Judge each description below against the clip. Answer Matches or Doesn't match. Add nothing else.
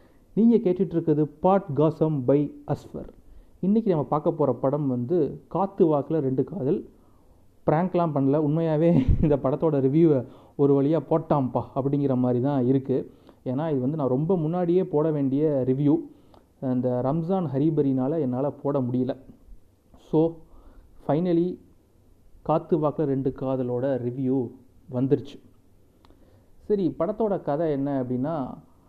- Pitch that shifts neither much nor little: Matches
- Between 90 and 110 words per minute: Doesn't match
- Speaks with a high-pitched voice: Doesn't match